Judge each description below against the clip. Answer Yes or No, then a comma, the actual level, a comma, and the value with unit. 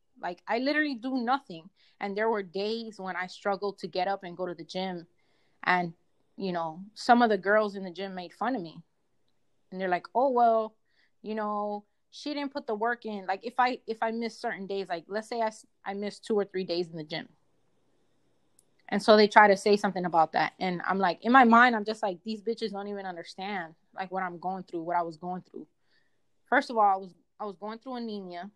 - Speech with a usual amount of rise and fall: Yes, average, 3.5 semitones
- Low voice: No, high, 200 Hz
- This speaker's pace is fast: Yes, fast, 235 wpm